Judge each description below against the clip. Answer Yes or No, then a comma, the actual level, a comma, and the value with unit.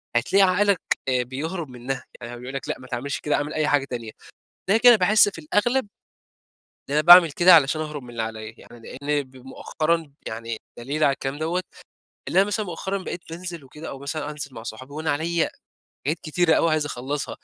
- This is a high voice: No, medium, 150 Hz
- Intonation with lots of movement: No, average, 4.5 semitones